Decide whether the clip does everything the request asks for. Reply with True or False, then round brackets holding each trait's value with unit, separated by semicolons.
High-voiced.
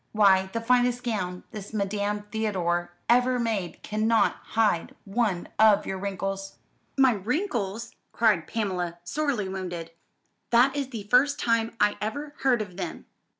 True (215 Hz)